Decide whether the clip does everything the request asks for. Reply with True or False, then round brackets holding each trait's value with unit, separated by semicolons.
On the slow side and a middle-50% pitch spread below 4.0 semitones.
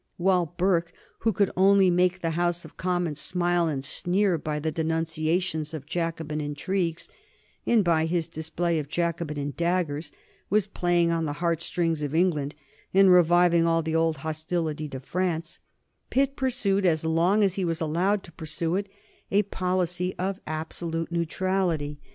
False (155 wpm; 2.4 semitones)